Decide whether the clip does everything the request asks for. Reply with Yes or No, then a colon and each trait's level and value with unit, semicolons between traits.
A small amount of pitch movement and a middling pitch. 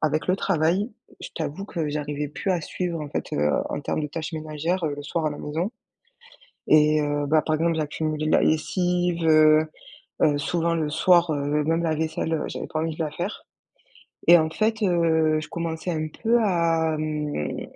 Yes: narrow, 2.0 semitones; medium, 160 Hz